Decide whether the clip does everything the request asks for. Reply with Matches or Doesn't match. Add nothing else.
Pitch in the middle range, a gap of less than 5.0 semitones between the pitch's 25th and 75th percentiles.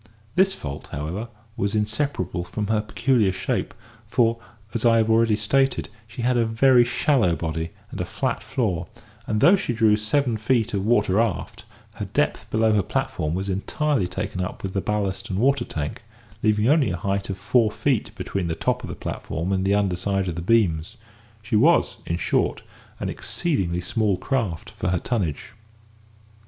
Doesn't match